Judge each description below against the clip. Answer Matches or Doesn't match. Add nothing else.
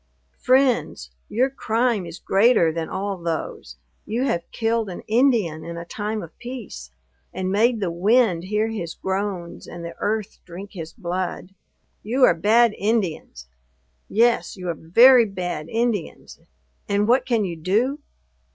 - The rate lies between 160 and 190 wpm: Doesn't match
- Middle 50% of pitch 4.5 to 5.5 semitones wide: Matches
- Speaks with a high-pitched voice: Matches